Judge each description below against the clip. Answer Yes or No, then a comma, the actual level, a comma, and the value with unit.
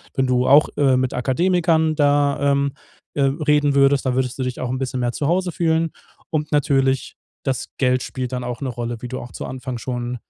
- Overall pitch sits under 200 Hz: Yes, low, 135 Hz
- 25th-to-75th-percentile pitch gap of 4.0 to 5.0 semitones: No, narrow, 2.5 semitones